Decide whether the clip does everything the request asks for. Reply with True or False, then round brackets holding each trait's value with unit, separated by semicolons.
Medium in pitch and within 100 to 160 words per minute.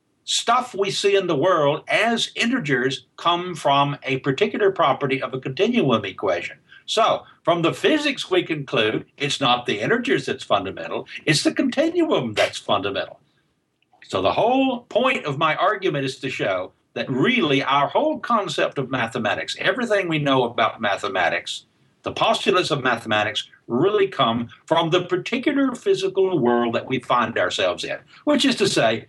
True (180 Hz; 155 wpm)